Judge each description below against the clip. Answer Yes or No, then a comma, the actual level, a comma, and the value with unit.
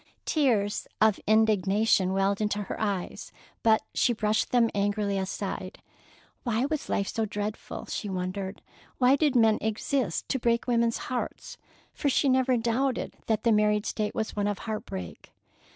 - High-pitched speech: Yes, high, 215 Hz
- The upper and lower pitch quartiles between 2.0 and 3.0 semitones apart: Yes, average, 2.7 semitones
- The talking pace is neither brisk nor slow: Yes, average, 150 wpm